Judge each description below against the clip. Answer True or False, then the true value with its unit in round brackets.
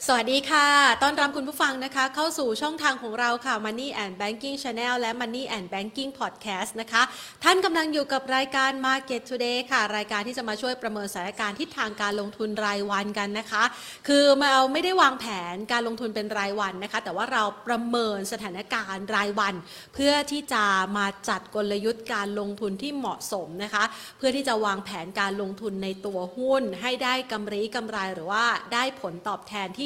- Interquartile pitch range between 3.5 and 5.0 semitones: True (4.4 semitones)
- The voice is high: True (225 Hz)